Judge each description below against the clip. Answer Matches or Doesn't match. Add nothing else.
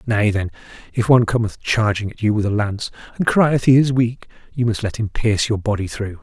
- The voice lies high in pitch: Doesn't match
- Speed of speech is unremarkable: Doesn't match